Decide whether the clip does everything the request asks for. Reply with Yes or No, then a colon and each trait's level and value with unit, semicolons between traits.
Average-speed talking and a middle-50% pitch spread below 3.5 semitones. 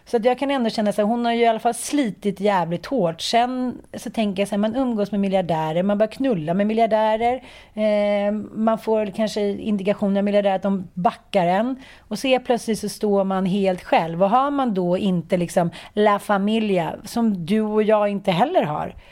No: fast, 210 wpm; average, 2.9 semitones